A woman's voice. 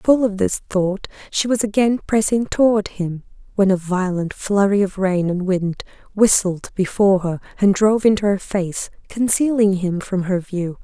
Yes: female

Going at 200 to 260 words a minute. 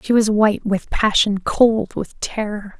No: average, 170 wpm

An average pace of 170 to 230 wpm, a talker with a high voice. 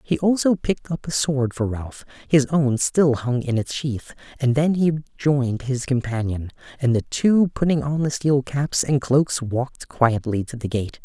No: average, 185 wpm; low, 135 Hz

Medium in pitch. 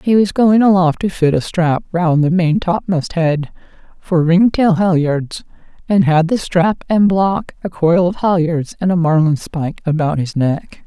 Yes: medium, 180 Hz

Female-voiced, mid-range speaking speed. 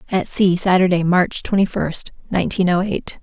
Yes: female; average, 165 wpm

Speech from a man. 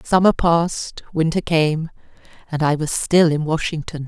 No: female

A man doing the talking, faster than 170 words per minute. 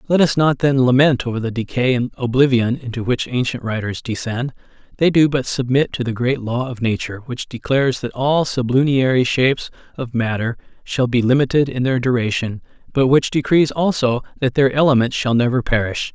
Yes: male; average, 180 wpm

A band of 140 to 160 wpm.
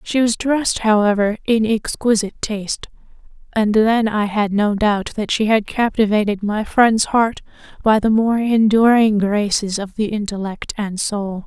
Yes: average, 150 wpm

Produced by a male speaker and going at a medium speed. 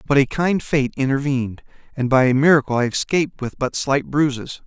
Yes: male; average, 195 wpm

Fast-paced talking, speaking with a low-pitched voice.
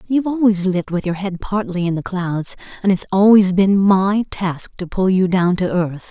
No: fast, 215 wpm; high, 190 Hz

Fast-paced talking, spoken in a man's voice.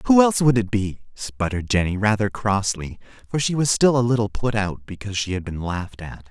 Yes: fast, 220 wpm; male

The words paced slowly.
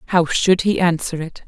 No: fast, 205 wpm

